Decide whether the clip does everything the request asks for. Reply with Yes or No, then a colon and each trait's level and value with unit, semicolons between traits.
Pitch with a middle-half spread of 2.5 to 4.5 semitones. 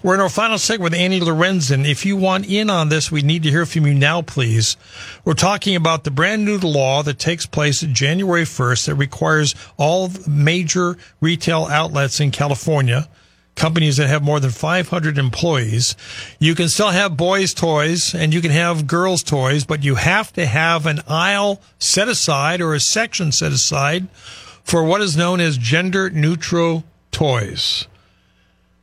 Yes: average, 3.8 semitones